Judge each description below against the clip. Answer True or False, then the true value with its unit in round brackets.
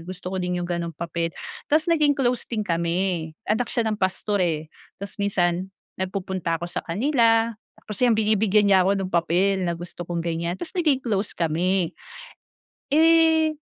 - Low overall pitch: False (190 Hz)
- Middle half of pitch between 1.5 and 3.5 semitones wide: False (4.7 semitones)